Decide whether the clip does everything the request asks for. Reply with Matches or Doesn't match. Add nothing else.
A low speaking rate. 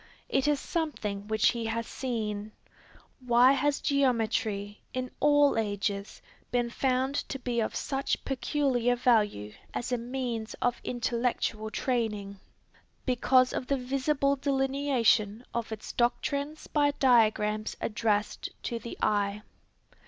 Matches